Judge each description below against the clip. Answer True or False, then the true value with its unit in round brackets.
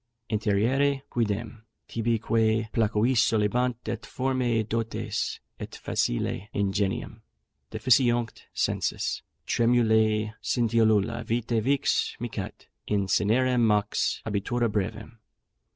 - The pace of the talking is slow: True (90 wpm)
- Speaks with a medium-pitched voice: False (115 Hz)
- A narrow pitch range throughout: True (2.0 semitones)